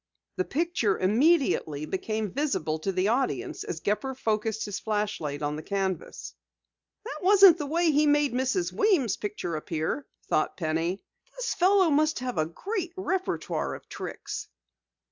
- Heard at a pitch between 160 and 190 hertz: No, high, 235 Hz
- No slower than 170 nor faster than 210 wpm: No, average, 145 wpm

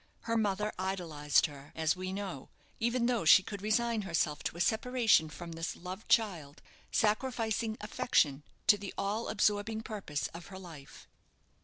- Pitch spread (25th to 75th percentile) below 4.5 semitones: No, average, 5.0 semitones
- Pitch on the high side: Yes, high, 195 Hz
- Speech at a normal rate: Yes, average, 155 wpm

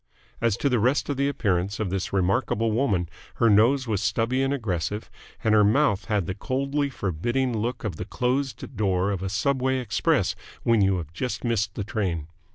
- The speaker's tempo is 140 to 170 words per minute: No, average, 190 wpm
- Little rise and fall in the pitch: No, average, 4.8 semitones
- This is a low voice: Yes, low, 110 Hz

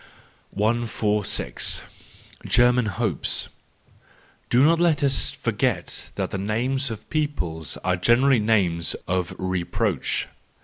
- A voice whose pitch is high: No, low, 110 Hz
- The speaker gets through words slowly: Yes, slow, 105 wpm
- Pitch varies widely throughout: Yes, wide, 6.0 semitones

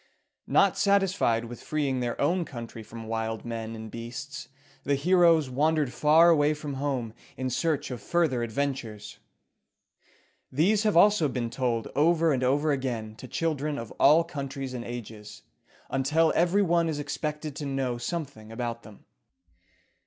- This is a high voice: No, medium, 140 Hz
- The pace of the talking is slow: No, average, 150 wpm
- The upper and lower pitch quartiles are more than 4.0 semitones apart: Yes, average, 5.1 semitones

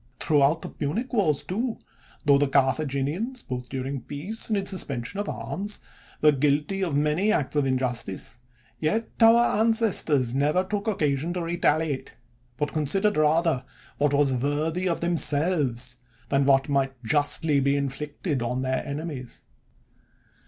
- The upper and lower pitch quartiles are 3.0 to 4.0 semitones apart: No, average, 4.8 semitones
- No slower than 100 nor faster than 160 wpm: Yes, average, 145 wpm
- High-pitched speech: No, medium, 150 Hz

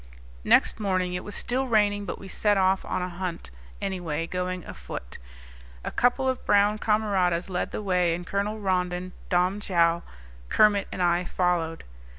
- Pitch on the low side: No, medium, 185 Hz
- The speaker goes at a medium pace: Yes, average, 165 wpm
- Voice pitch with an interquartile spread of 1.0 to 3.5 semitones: Yes, narrow, 2.6 semitones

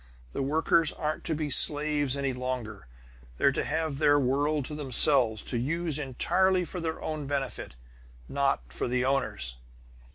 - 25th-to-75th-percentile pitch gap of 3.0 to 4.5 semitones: Yes, average, 3.3 semitones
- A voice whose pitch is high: No, medium, 140 Hz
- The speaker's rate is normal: Yes, average, 155 wpm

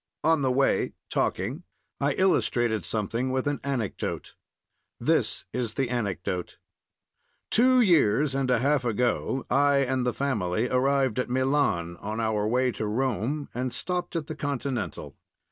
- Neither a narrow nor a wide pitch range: Yes, average, 4.0 semitones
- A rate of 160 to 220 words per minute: No, average, 145 wpm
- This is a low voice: Yes, low, 130 Hz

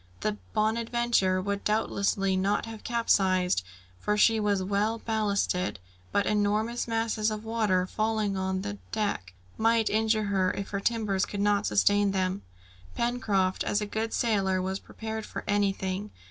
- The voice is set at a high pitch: Yes, high, 205 Hz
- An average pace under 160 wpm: Yes, average, 145 wpm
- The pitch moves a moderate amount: No, narrow, 2.3 semitones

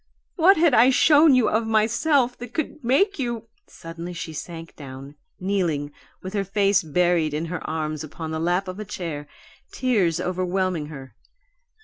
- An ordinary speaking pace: Yes, average, 165 wpm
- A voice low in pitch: No, medium, 185 Hz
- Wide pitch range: Yes, wide, 6.7 semitones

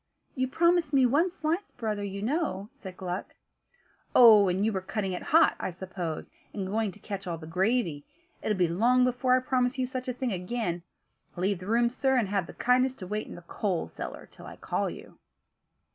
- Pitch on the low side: No, high, 215 Hz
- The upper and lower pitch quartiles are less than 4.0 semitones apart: No, average, 5.2 semitones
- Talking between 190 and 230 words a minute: Yes, fast, 205 wpm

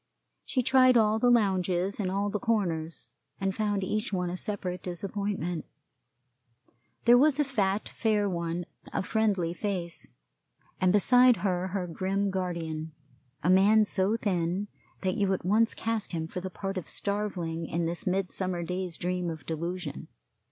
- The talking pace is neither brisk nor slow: Yes, average, 155 wpm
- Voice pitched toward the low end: No, high, 190 Hz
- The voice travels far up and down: No, average, 3.0 semitones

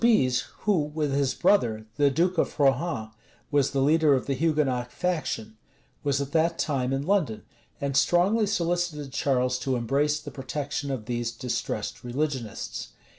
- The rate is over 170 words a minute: No, average, 155 wpm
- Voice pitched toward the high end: No, medium, 140 Hz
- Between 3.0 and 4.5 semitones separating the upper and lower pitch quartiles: Yes, average, 4.0 semitones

